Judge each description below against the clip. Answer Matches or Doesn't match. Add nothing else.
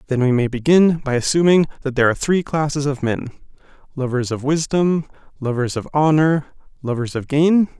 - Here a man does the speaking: Matches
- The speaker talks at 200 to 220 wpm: Doesn't match